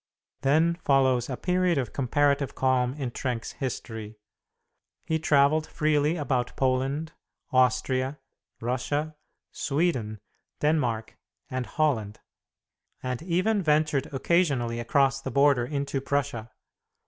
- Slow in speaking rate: Yes, slow, 105 wpm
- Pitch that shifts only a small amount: No, average, 3.2 semitones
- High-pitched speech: No, low, 135 Hz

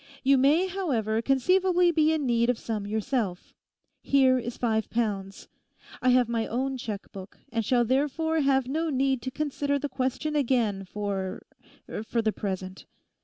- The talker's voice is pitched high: Yes, very high, 255 Hz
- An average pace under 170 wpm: Yes, average, 155 wpm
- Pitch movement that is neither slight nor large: Yes, average, 4.4 semitones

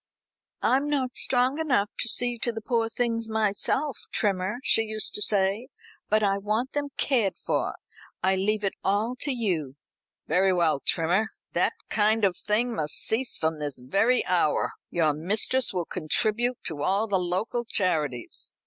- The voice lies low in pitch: No, high, 210 Hz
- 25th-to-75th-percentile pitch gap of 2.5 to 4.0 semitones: No, average, 4.6 semitones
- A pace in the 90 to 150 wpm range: No, average, 160 wpm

